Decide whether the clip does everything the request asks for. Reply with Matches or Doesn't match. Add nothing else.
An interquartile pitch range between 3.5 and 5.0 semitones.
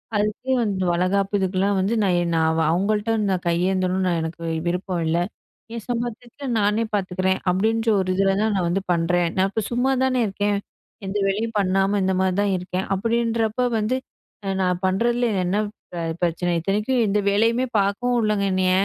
Doesn't match